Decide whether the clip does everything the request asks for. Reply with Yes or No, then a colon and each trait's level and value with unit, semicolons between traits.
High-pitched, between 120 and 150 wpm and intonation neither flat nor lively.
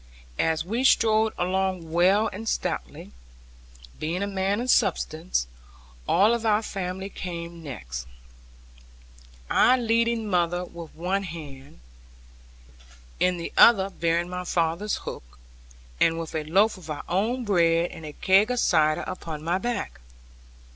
No: medium, 180 Hz; slow, 135 wpm; average, 4.0 semitones